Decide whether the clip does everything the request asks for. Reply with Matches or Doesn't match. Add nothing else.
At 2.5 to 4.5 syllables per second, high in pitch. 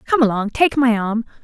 Doesn't match